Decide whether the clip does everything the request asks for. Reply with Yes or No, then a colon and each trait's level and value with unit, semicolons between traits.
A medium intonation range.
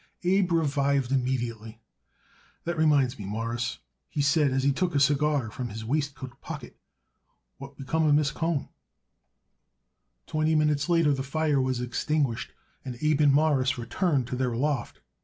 Yes: average, 3.3 semitones